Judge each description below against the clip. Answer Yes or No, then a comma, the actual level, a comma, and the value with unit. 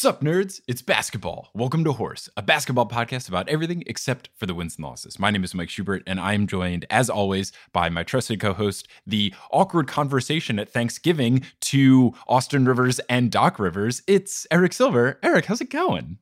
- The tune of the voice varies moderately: No, wide, 6.4 semitones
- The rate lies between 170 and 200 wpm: Yes, average, 195 wpm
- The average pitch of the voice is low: Yes, low, 125 Hz